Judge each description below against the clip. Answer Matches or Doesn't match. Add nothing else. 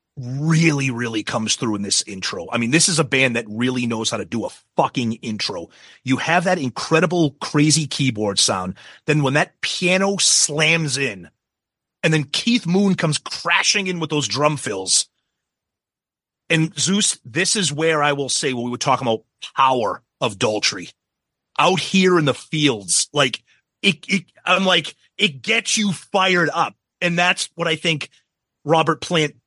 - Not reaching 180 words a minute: Matches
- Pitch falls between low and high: Matches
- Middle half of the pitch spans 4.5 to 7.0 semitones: Matches